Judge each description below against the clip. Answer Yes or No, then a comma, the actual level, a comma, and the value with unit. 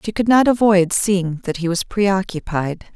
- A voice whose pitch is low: No, high, 190 Hz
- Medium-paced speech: Yes, average, 185 wpm